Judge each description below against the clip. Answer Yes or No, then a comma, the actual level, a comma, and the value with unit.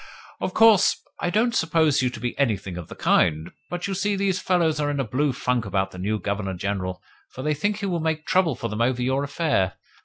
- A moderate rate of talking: No, fast, 235 wpm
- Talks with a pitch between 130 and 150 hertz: Yes, low, 135 Hz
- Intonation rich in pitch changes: Yes, wide, 8.8 semitones